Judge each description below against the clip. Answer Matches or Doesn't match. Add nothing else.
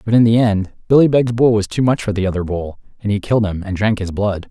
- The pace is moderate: Doesn't match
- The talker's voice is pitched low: Matches